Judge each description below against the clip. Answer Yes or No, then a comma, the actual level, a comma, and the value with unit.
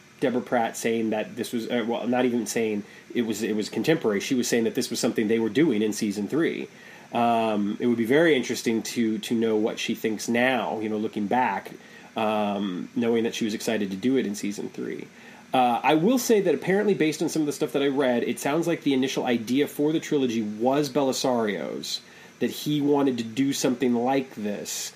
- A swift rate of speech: Yes, fast, 220 wpm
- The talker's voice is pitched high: No, low, 120 Hz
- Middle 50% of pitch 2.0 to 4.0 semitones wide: No, average, 4.4 semitones